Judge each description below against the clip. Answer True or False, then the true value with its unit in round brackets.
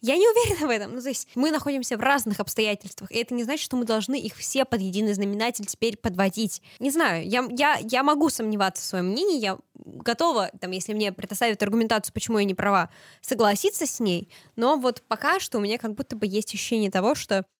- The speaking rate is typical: False (215 wpm)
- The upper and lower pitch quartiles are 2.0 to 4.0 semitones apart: False (4.5 semitones)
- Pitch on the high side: True (225 Hz)